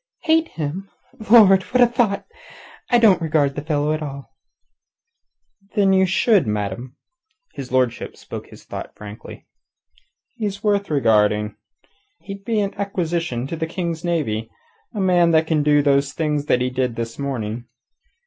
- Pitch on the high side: No, medium, 155 Hz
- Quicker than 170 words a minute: No, average, 150 wpm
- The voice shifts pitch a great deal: Yes, wide, 7.1 semitones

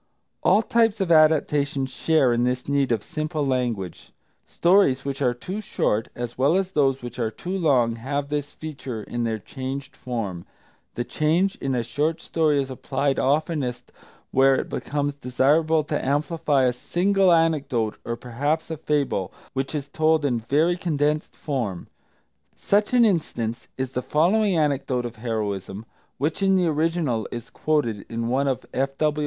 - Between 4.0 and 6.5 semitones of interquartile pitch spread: Yes, average, 4.3 semitones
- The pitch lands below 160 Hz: Yes, medium, 140 Hz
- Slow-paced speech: No, average, 160 wpm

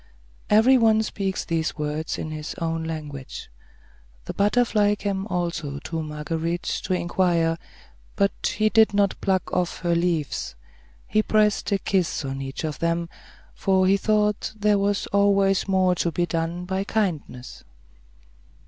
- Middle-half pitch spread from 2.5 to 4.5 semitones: Yes, average, 3.7 semitones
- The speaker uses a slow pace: No, average, 145 wpm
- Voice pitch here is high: No, medium, 180 Hz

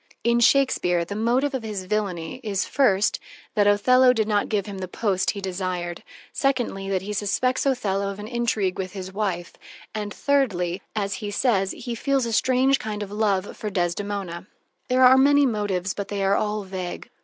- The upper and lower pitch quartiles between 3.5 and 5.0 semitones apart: Yes, average, 3.9 semitones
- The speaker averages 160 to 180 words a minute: No, average, 190 wpm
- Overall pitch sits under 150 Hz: No, high, 205 Hz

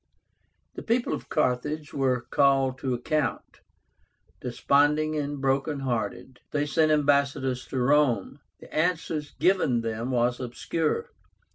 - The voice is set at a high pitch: No, medium, 140 Hz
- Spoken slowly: Yes, slow, 120 wpm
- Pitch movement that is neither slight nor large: Yes, average, 3.1 semitones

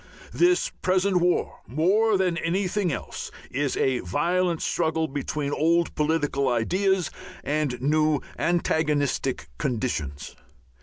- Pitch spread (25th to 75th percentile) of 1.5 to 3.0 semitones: No, average, 4.4 semitones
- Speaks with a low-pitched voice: No, medium, 160 Hz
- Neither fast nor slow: No, slow, 105 wpm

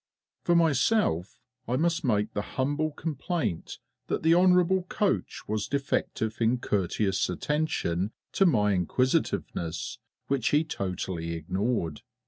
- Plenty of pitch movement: Yes, wide, 8.9 semitones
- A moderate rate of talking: No, slow, 115 wpm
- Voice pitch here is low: Yes, low, 125 Hz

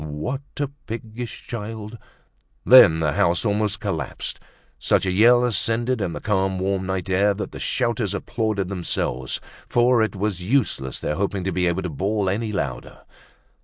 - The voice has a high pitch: No, low, 100 Hz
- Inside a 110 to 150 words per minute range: No, average, 165 wpm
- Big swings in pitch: No, average, 3.6 semitones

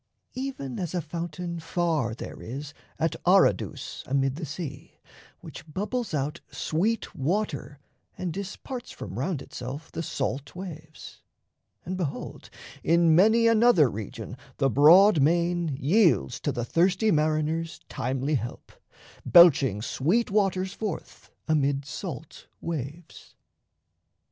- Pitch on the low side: No, medium, 160 Hz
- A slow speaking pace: Yes, slow, 120 wpm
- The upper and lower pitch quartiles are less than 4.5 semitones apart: No, average, 4.8 semitones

